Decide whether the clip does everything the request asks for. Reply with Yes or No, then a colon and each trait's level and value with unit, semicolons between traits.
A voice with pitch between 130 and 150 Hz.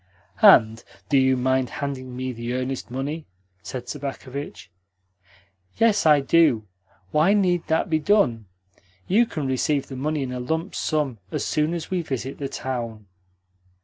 Yes: low, 135 Hz